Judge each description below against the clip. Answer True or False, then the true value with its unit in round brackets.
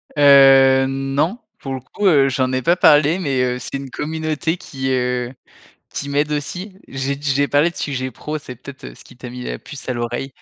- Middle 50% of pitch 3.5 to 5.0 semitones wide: False (2.4 semitones)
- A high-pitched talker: False (135 Hz)